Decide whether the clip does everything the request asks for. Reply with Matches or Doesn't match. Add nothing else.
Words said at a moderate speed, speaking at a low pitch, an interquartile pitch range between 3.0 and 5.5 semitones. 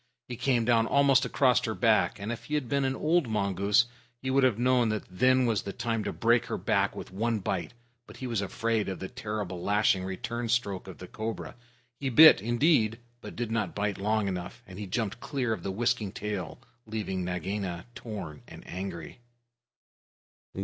Matches